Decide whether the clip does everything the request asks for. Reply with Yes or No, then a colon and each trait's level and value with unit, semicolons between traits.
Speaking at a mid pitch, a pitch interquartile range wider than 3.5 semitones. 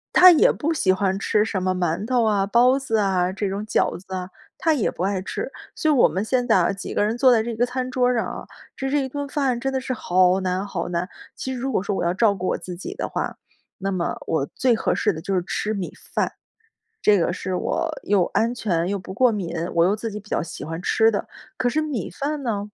No: high, 210 Hz; average, 5.1 semitones